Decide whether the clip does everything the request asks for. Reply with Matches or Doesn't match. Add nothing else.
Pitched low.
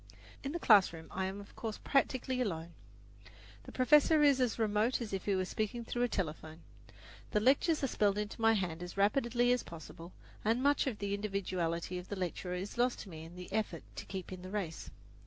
Doesn't match